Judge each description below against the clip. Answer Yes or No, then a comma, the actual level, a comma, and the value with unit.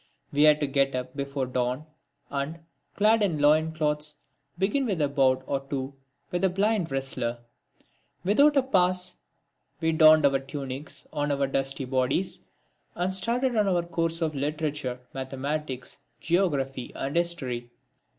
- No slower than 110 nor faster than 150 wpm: Yes, average, 145 wpm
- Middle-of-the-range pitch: Yes, medium, 150 Hz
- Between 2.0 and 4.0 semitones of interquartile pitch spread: No, average, 4.5 semitones